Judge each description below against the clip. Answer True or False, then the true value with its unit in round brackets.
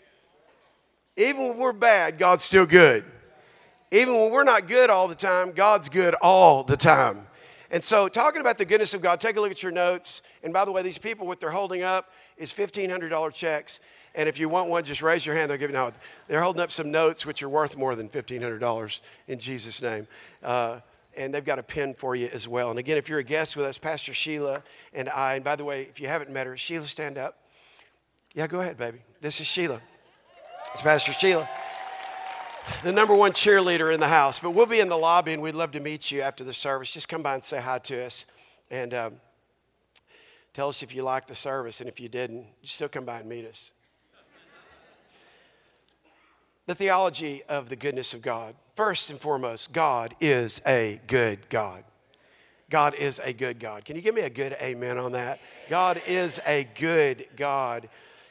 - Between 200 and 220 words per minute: True (205 wpm)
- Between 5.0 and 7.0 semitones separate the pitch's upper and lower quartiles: True (5.6 semitones)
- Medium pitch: True (150 Hz)